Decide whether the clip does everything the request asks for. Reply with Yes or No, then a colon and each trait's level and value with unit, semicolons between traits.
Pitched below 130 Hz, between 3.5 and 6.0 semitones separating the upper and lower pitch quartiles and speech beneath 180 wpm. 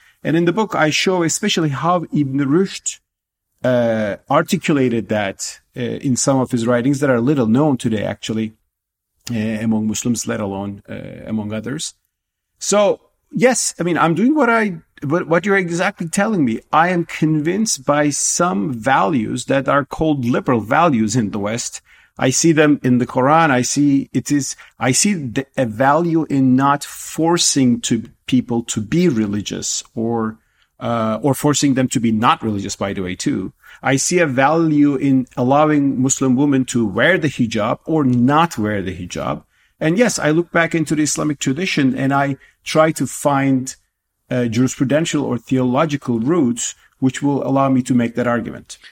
No: low, 135 Hz; average, 5.0 semitones; average, 170 wpm